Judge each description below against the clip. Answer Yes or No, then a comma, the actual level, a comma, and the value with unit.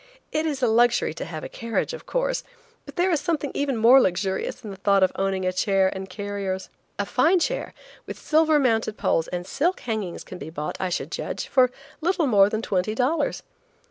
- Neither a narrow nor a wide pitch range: No, wide, 7.1 semitones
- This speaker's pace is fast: Yes, fast, 210 wpm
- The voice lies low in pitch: No, high, 220 Hz